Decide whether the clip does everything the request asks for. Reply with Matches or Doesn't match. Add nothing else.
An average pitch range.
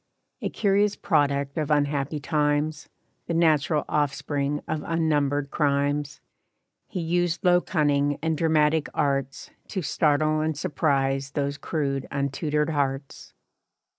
Doesn't match